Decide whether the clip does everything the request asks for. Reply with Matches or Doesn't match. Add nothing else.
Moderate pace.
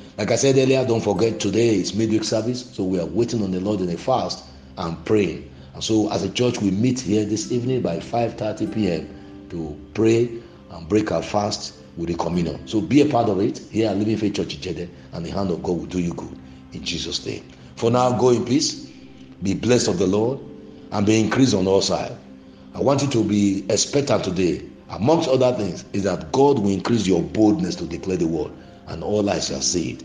Doesn't match